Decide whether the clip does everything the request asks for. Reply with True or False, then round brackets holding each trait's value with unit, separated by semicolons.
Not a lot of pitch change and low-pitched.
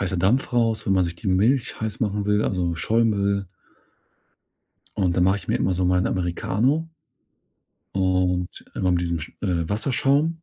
False (3.7 semitones; 95 Hz)